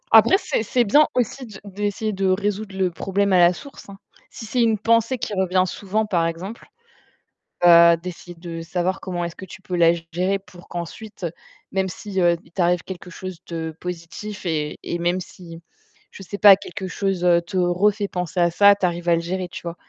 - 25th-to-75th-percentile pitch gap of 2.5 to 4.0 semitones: Yes, average, 2.8 semitones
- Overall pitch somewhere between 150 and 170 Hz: No, medium, 185 Hz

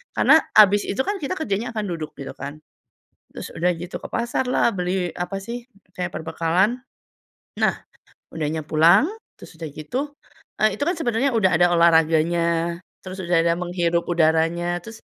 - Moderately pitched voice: Yes, medium, 175 Hz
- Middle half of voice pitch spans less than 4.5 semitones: No, average, 5.0 semitones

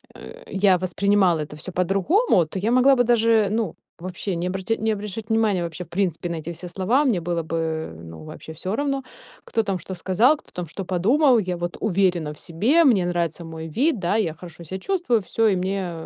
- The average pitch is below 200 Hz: Yes, medium, 185 Hz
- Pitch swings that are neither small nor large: Yes, average, 4.5 semitones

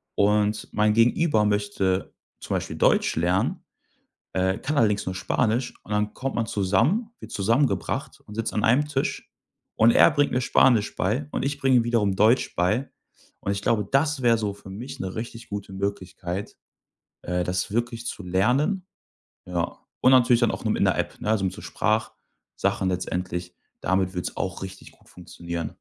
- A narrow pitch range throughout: No, average, 4.1 semitones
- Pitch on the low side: Yes, low, 105 Hz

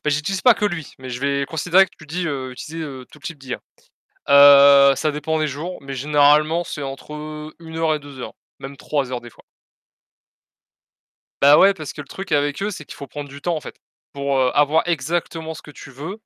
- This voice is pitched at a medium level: Yes, medium, 150 Hz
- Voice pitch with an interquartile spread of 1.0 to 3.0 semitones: Yes, narrow, 2.6 semitones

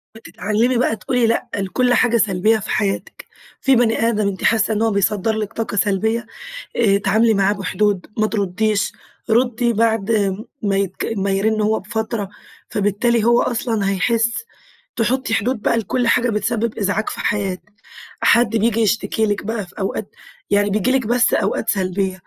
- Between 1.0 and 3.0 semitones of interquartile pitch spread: Yes, narrow, 2.4 semitones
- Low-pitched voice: No, high, 215 Hz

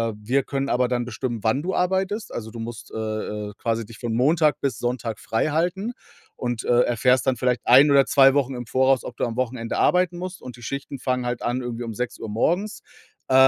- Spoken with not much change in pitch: No, average, 3.2 semitones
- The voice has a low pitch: Yes, low, 125 Hz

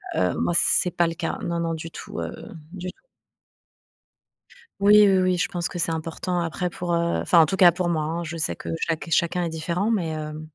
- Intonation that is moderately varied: No, narrow, 1.7 semitones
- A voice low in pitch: No, medium, 170 Hz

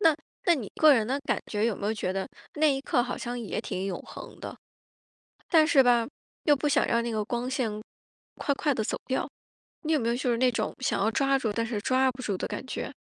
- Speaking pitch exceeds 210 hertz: Yes, high, 245 Hz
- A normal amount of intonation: Yes, average, 3.7 semitones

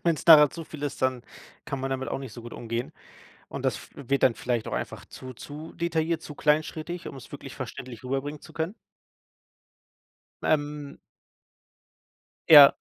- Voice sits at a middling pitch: Yes, medium, 145 Hz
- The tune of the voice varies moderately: Yes, average, 3.2 semitones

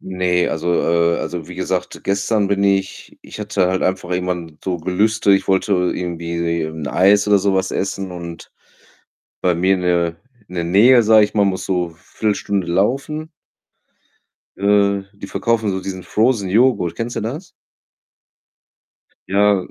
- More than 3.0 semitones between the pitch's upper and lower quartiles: No, narrow, 2.6 semitones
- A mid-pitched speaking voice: No, very low, 95 Hz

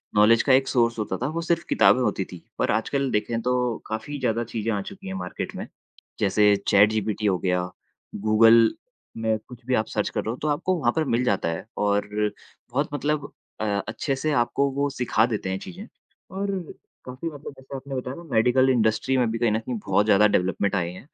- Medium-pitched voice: No, low, 115 Hz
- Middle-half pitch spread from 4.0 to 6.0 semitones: Yes, average, 4.3 semitones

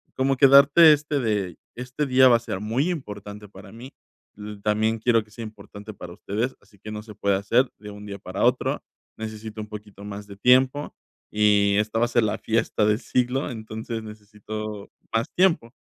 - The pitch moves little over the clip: No, average, 3.2 semitones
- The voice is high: No, low, 110 Hz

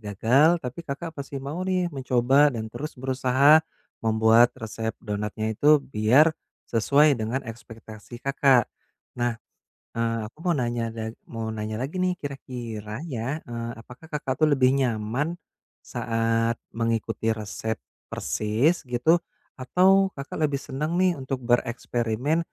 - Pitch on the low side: Yes, low, 125 Hz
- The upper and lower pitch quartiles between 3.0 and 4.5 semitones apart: Yes, average, 4.1 semitones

